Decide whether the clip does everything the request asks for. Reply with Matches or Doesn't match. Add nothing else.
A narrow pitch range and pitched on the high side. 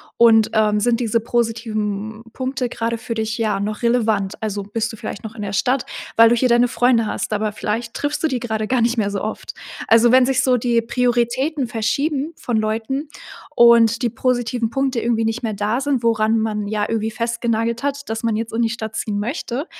Matches